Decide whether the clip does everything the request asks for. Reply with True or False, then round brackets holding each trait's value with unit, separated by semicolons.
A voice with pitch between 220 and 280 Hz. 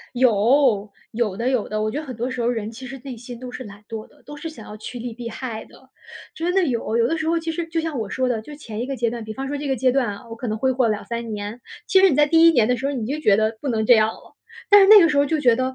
True (245 Hz)